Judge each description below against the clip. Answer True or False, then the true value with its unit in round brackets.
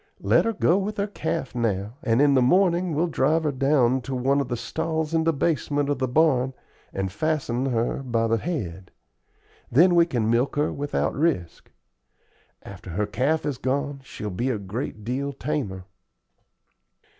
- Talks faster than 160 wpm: True (175 wpm)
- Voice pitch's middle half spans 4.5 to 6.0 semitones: True (5.2 semitones)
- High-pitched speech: False (135 Hz)